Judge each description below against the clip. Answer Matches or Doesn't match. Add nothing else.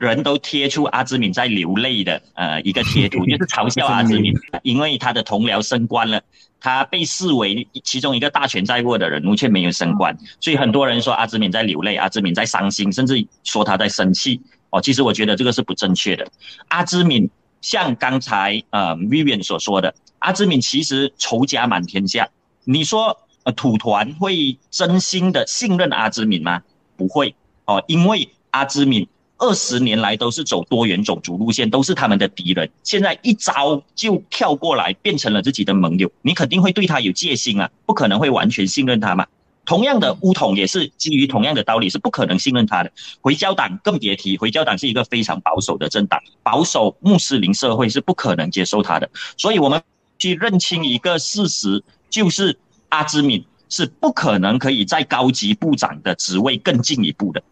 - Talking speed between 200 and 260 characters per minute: Doesn't match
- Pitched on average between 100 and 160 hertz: Matches